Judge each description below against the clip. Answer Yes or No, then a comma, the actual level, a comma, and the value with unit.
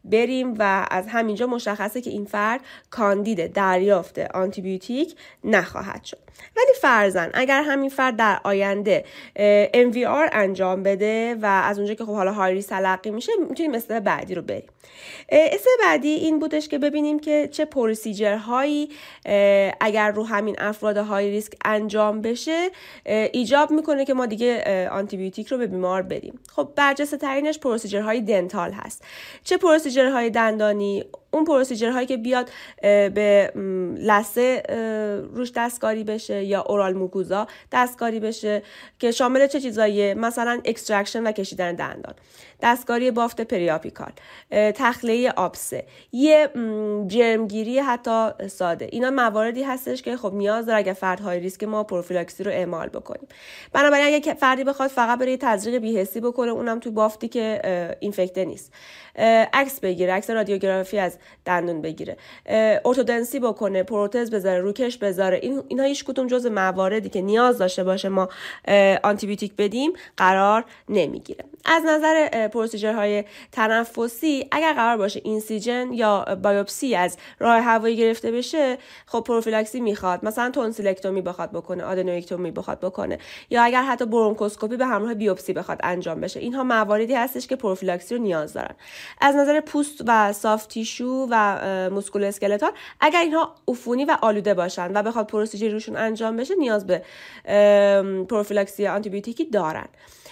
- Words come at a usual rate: Yes, average, 145 wpm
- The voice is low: No, high, 220 Hz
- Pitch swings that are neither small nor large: Yes, average, 4.0 semitones